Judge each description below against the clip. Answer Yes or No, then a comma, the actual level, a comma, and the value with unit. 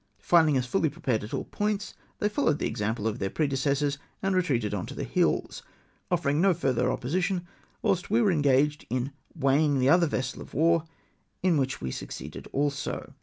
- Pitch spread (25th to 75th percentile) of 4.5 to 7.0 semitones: Yes, average, 5.0 semitones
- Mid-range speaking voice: Yes, medium, 145 Hz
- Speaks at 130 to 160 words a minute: No, average, 175 wpm